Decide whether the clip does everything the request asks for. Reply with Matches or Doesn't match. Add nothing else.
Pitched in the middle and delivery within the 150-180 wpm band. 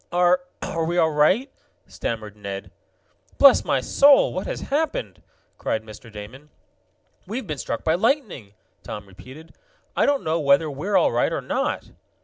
Matches